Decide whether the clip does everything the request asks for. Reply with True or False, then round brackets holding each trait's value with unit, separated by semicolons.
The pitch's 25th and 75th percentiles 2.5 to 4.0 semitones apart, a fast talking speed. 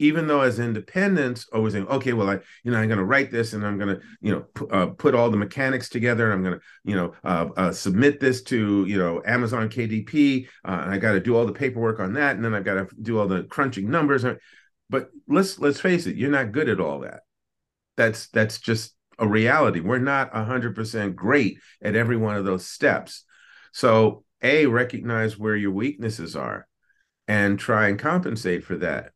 True (3.6 semitones; 220 wpm)